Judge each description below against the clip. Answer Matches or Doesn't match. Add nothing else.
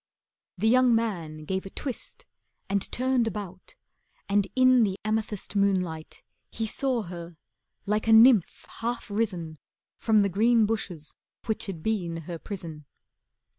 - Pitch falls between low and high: Doesn't match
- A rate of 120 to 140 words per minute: Matches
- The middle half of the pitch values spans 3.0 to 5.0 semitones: Matches